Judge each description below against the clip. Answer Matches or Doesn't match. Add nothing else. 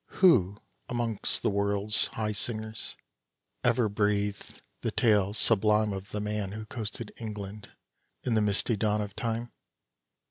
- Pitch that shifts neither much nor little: Doesn't match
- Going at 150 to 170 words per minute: Doesn't match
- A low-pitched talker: Matches